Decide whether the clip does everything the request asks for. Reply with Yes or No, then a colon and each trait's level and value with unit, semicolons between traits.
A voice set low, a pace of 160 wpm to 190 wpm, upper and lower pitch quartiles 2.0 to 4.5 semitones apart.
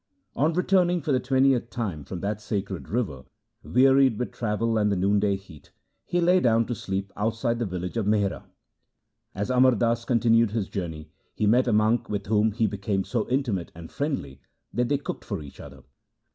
Yes: low, 110 Hz; average, 185 wpm; average, 4.1 semitones